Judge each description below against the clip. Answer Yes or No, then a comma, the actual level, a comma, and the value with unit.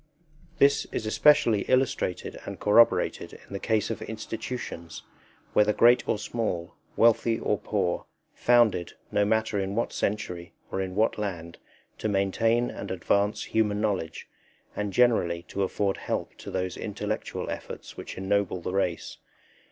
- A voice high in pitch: No, low, 105 Hz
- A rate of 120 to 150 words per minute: Yes, average, 145 wpm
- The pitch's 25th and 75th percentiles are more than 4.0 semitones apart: No, average, 2.8 semitones